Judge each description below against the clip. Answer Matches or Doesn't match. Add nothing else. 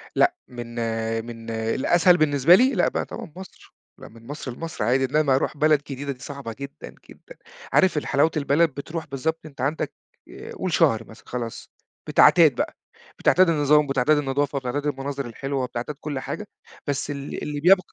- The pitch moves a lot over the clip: Doesn't match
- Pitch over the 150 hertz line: Doesn't match